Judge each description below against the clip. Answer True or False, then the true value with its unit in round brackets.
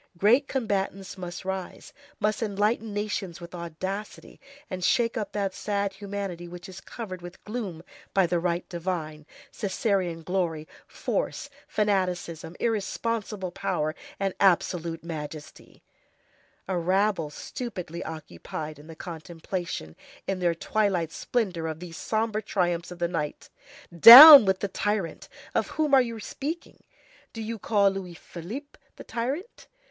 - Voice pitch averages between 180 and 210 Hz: True (190 Hz)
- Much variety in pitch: False (3.7 semitones)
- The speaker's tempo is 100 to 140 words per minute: True (135 wpm)